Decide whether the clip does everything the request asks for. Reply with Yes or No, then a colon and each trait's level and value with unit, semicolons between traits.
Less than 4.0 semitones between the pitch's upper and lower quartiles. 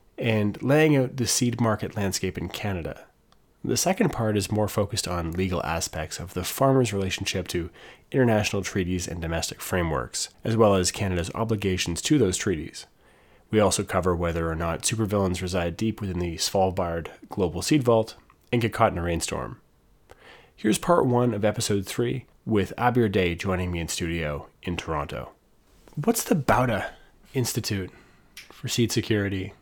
No: average, 4.5 semitones